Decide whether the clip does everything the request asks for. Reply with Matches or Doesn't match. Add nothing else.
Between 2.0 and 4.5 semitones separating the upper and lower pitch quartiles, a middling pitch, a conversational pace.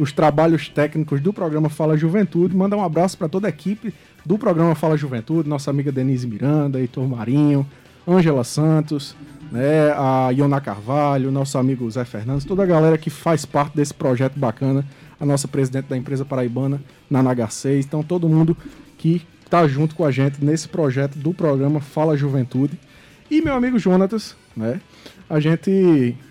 Matches